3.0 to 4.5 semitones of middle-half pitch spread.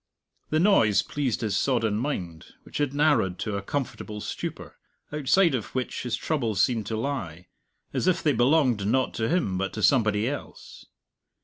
No: wide, 5.5 semitones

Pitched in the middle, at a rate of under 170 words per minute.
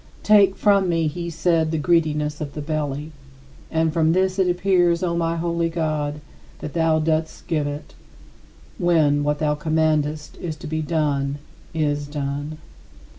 Yes: medium, 160 Hz; average, 150 wpm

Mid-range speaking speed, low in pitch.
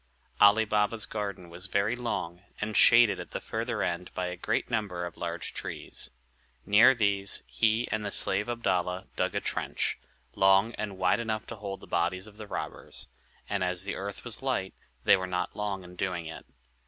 Yes: average, 190 wpm; low, 100 Hz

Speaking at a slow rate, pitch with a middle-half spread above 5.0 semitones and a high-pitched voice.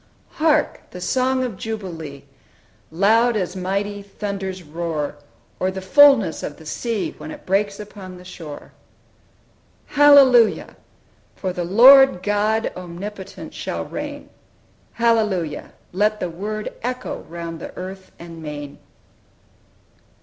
No: slow, 120 wpm; average, 4.3 semitones; high, 195 Hz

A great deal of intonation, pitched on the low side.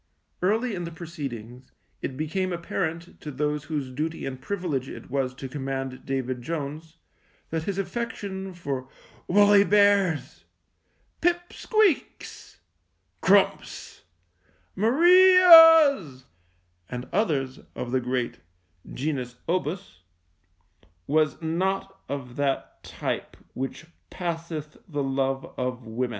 No: wide, 6.5 semitones; medium, 155 Hz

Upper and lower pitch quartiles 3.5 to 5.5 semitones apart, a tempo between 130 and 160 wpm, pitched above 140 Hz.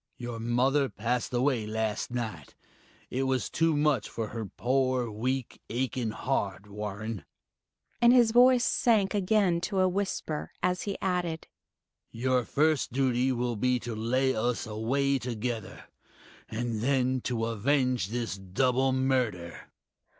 No: average, 3.8 semitones; slow, 135 wpm; low, 125 Hz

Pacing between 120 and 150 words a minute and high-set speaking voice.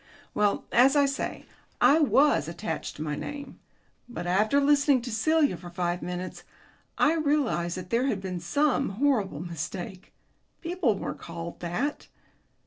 Yes: average, 145 wpm; high, 220 Hz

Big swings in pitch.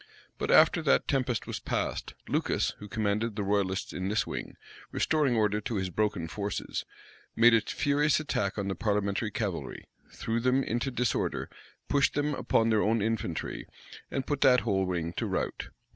No: average, 3.8 semitones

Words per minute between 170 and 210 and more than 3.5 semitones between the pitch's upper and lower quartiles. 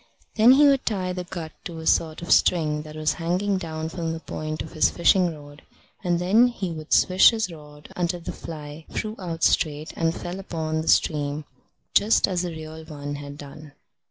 No: average, 200 wpm; average, 2.9 semitones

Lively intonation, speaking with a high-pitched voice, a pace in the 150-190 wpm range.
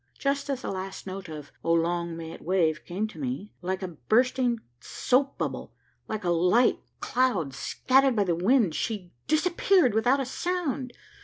Yes: wide, 6.9 semitones; high, 215 Hz; average, 170 wpm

